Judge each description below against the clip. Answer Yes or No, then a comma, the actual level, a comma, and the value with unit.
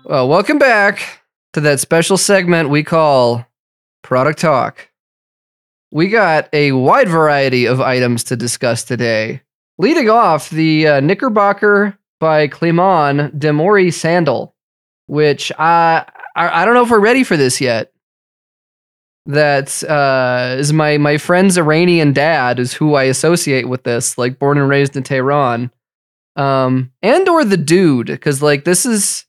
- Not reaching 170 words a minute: Yes, average, 145 wpm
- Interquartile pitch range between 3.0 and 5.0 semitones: Yes, average, 4.7 semitones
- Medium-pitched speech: Yes, medium, 150 Hz